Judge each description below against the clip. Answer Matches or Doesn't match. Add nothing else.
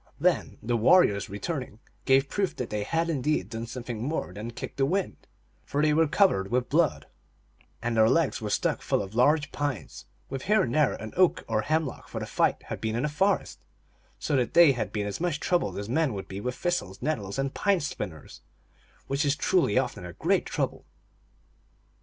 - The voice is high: Doesn't match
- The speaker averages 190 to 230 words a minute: Matches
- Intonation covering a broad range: Matches